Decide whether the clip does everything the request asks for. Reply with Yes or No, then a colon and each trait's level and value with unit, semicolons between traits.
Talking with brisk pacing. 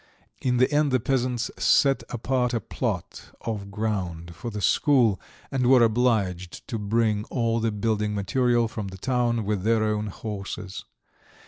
No: average, 155 wpm